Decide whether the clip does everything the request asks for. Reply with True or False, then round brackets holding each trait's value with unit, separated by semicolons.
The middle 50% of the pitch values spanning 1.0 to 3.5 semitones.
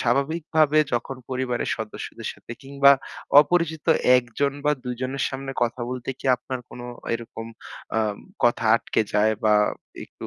True (2.8 semitones)